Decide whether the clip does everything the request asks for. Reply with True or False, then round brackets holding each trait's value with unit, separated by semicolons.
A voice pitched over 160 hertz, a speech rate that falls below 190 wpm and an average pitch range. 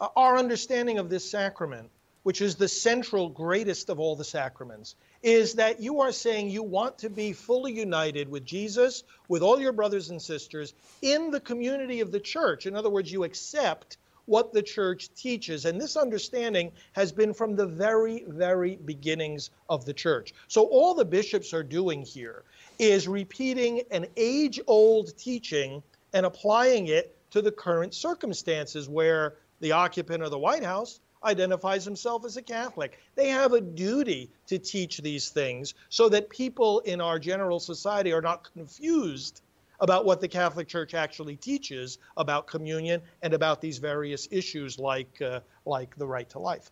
False (190 Hz; 170 wpm; 6.3 semitones)